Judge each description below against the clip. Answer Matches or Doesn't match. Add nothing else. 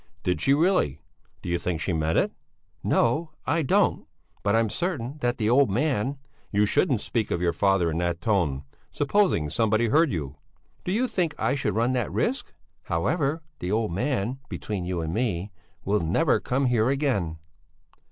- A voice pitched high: Doesn't match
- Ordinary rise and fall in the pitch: Doesn't match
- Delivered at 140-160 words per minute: Doesn't match